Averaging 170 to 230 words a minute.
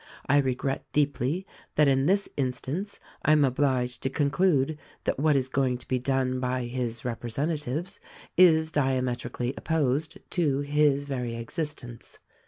No: average, 145 wpm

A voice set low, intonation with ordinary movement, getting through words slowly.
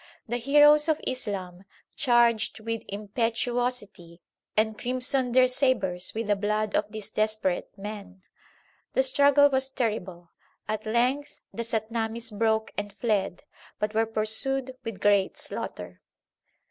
No: high, 225 Hz; average, 3.5 semitones; slow, 125 wpm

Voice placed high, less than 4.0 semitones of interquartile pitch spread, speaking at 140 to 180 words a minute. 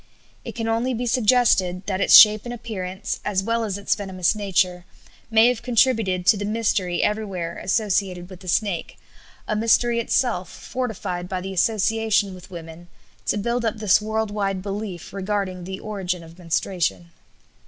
Yes: high, 200 Hz; average, 3.3 semitones; average, 165 wpm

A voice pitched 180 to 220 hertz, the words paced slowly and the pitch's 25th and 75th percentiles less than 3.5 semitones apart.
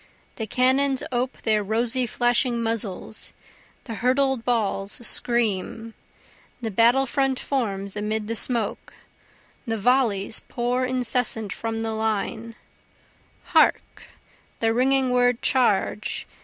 No: high, 230 Hz; slow, 110 wpm; narrow, 2.5 semitones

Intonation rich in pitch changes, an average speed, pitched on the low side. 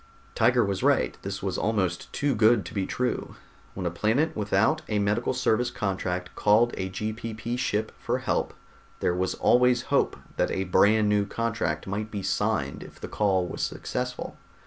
No: average, 3.5 semitones; average, 170 wpm; low, 105 Hz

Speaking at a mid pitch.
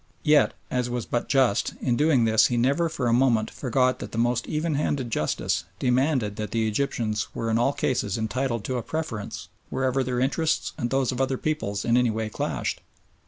No: low, 125 Hz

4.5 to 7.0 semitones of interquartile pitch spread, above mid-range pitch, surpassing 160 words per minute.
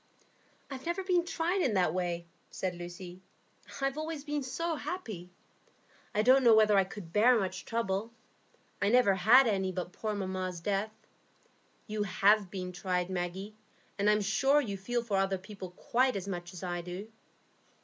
Yes: average, 4.9 semitones; high, 200 Hz; average, 170 wpm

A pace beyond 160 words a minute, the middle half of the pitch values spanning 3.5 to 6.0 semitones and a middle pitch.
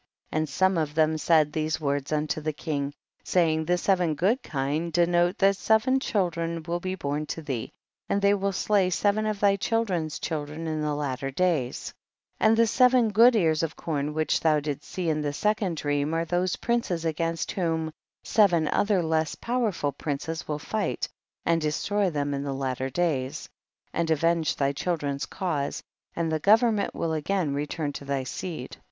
Yes: average, 185 wpm; average, 4.1 semitones; medium, 165 Hz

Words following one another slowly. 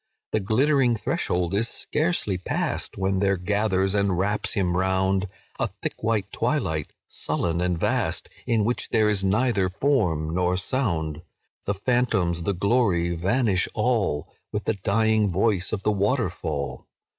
No: average, 145 wpm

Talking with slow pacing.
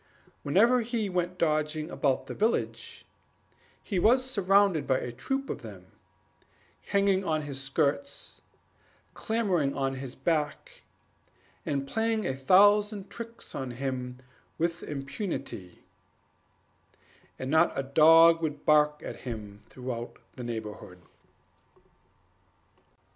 Yes: slow, 110 wpm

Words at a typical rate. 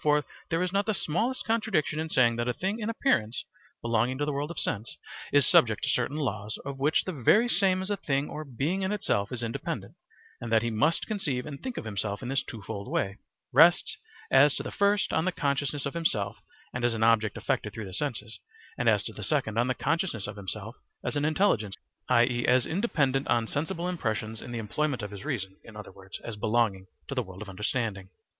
No: fast, 220 wpm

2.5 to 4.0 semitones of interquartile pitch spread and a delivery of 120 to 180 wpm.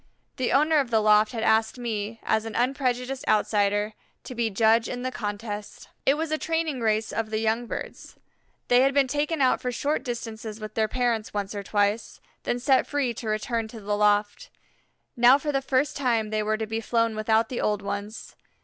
No: average, 3.0 semitones; fast, 205 wpm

